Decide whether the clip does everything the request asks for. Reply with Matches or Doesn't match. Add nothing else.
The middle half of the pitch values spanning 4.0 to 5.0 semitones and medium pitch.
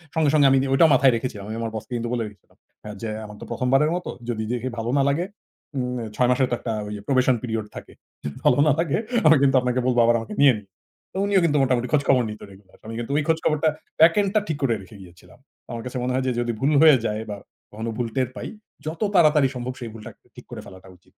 Doesn't match